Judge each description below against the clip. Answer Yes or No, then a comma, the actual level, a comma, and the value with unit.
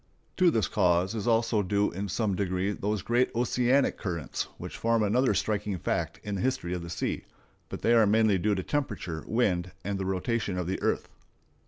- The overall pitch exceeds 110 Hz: No, low, 105 Hz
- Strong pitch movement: No, average, 3.8 semitones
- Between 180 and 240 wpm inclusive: Yes, average, 195 wpm